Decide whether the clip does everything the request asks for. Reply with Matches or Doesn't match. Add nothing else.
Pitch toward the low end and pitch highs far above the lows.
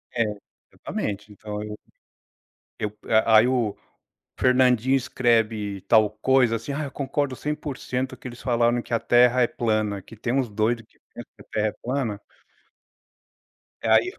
Doesn't match